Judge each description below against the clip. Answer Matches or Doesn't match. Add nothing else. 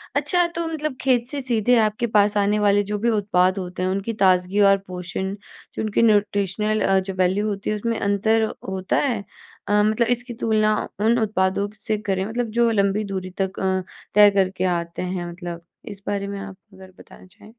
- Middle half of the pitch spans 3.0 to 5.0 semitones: Doesn't match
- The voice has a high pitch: Matches